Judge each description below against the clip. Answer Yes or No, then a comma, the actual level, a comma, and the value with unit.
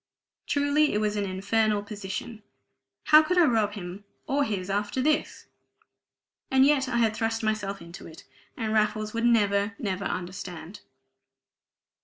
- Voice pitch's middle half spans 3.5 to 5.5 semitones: No, average, 3.0 semitones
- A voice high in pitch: Yes, high, 215 Hz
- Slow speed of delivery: No, average, 145 wpm